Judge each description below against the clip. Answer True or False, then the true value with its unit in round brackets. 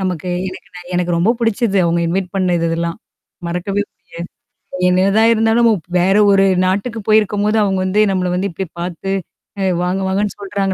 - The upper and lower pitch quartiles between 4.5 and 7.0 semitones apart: False (2.4 semitones)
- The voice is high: True (195 Hz)